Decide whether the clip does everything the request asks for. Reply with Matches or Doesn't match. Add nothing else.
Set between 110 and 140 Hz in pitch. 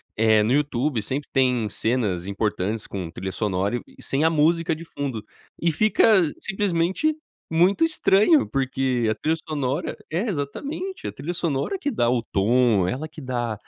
Matches